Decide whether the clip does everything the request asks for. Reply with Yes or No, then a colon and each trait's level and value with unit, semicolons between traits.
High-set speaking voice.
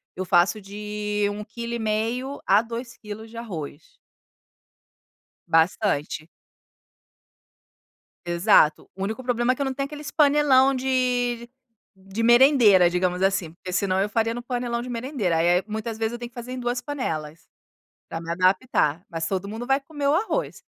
Yes: high, 225 Hz